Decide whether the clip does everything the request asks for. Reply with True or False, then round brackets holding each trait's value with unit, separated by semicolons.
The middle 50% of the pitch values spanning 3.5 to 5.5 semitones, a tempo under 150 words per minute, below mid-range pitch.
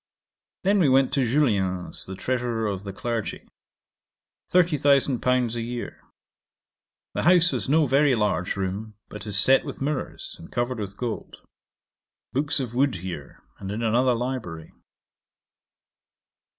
True (5.0 semitones; 135 wpm; 120 Hz)